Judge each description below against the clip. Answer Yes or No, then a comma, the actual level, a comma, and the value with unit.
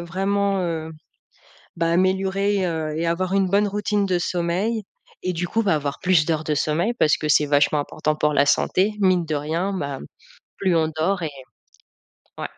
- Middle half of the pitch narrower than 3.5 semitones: No, average, 3.8 semitones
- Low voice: No, medium, 175 Hz